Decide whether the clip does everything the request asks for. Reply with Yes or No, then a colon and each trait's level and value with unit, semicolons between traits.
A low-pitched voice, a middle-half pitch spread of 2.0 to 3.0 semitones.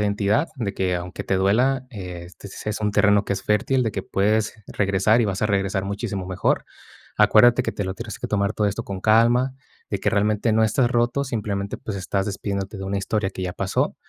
Yes: low, 105 Hz; narrow, 2.4 semitones